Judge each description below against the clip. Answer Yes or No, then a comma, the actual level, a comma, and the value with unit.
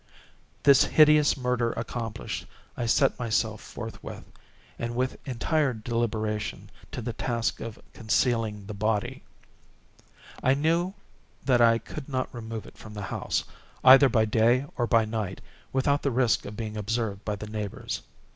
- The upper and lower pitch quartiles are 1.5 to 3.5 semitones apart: Yes, average, 2.9 semitones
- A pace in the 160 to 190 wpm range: No, average, 145 wpm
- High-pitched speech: No, low, 115 Hz